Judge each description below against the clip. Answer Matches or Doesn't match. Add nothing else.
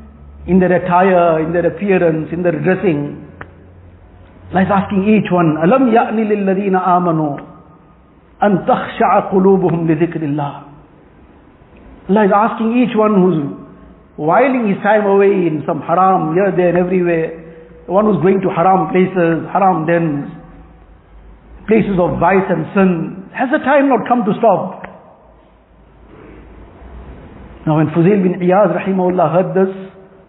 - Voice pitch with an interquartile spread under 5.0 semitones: Matches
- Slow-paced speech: Matches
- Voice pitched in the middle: Matches